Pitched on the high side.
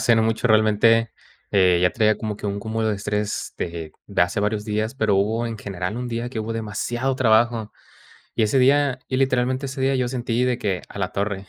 No: low, 110 Hz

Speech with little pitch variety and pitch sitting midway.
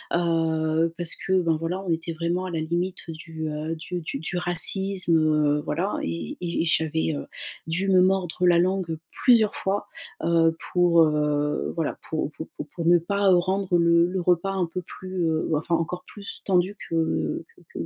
Yes: narrow, 2.3 semitones; medium, 170 Hz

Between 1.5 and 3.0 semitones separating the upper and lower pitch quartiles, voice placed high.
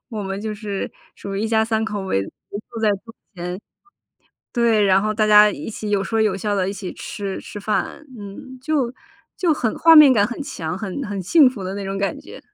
Yes: narrow, 2.6 semitones; high, 210 Hz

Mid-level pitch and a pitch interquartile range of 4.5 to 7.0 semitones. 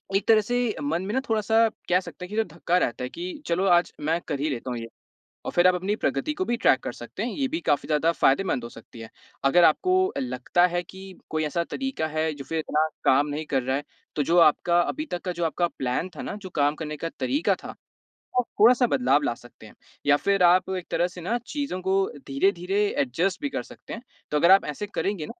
Yes: medium, 175 Hz; average, 5.3 semitones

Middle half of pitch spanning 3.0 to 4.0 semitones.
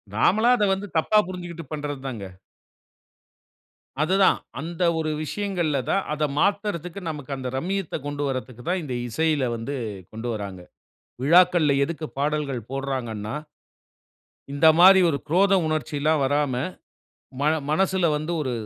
No: average, 4.6 semitones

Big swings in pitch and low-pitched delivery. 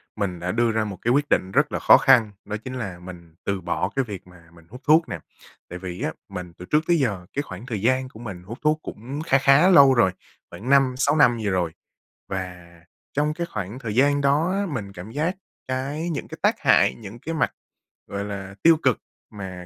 Yes: wide, 6.7 semitones; low, 115 Hz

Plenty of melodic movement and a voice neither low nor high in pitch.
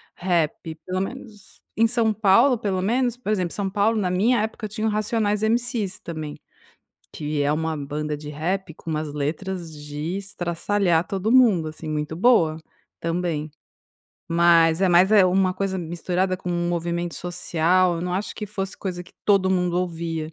No: average, 3.8 semitones; medium, 180 Hz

